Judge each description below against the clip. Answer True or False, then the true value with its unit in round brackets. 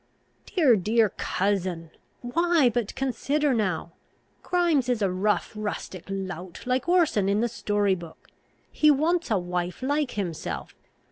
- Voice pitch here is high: True (215 Hz)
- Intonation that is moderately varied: False (6.6 semitones)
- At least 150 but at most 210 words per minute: False (135 wpm)